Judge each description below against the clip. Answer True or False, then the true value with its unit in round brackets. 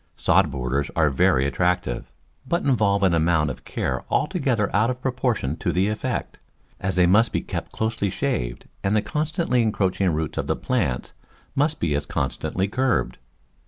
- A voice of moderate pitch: False (100 Hz)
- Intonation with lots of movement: True (7.6 semitones)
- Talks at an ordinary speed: True (165 wpm)